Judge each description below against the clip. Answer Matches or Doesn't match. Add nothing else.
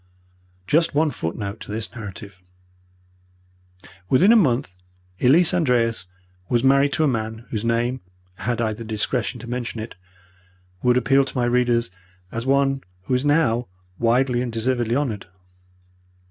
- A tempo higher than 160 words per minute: Doesn't match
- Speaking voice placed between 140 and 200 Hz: Doesn't match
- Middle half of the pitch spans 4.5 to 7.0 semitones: Doesn't match